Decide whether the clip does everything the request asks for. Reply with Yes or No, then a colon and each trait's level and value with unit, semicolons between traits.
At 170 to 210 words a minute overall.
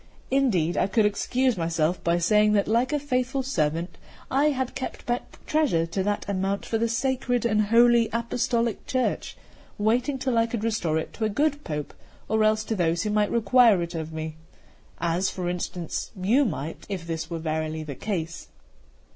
Yes: average, 180 wpm